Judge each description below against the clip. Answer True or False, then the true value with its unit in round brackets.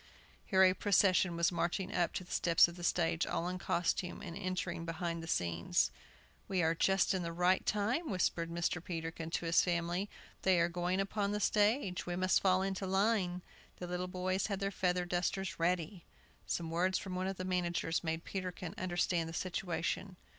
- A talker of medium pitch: True (180 Hz)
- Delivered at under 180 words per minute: False (185 wpm)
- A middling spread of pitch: False (1.9 semitones)